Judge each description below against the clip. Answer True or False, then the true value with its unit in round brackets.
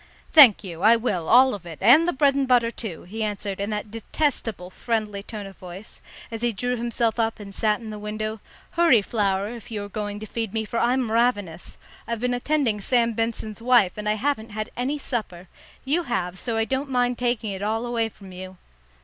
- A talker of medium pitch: False (225 Hz)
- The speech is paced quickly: True (215 wpm)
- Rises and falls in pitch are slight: False (3.0 semitones)